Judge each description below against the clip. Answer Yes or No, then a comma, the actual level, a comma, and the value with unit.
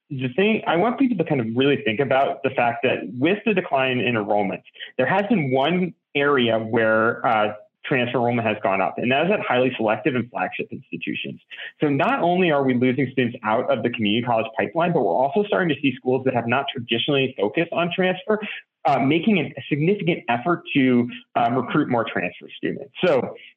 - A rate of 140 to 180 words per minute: No, average, 200 wpm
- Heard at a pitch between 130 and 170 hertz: Yes, low, 135 Hz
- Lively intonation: Yes, wide, 6.0 semitones